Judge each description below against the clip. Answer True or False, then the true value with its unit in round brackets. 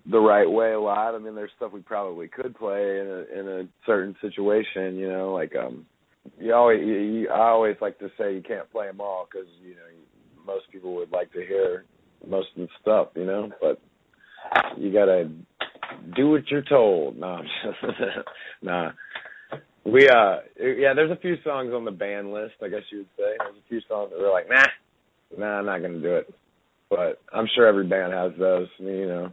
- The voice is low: True (110 Hz)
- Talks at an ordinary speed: False (210 wpm)